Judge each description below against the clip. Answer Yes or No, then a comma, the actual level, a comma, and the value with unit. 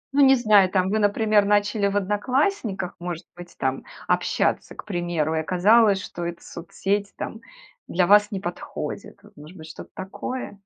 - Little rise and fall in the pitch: No, average, 3.2 semitones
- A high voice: Yes, high, 195 Hz